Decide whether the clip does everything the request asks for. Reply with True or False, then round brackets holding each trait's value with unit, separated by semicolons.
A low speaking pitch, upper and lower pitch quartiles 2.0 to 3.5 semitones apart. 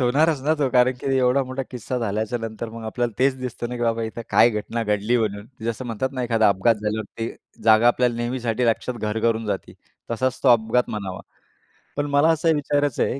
True (120 Hz; 2.6 semitones)